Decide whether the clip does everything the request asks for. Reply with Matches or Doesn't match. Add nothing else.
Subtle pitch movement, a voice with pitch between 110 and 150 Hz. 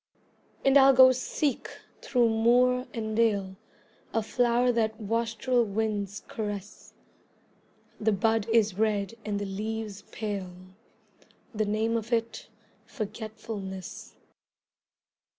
Doesn't match